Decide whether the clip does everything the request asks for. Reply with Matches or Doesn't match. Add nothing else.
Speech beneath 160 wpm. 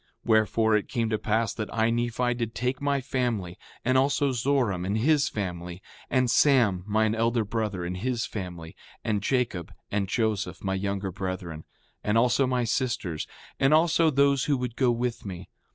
Doesn't match